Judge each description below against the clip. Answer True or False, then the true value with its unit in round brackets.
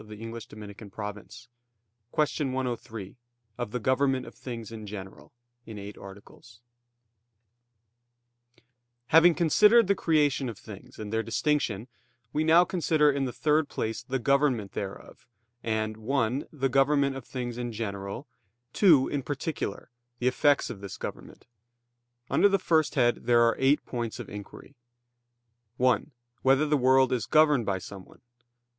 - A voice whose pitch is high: False (125 Hz)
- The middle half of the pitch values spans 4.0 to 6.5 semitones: True (5.0 semitones)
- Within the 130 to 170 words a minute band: True (140 wpm)